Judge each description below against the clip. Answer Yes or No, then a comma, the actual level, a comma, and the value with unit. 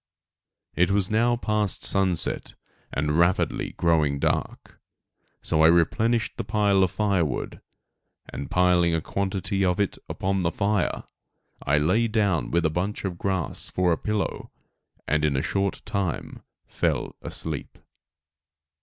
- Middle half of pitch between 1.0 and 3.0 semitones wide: No, average, 3.5 semitones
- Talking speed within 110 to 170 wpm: Yes, slow, 135 wpm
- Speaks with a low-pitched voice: Yes, very low, 95 Hz